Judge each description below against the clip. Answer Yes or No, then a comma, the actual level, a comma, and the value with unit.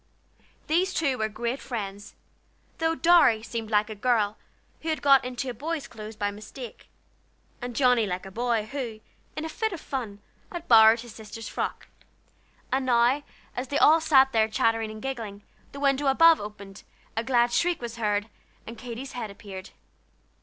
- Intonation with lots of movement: No, average, 4.1 semitones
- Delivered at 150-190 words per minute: Yes, average, 170 wpm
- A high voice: Yes, high, 240 Hz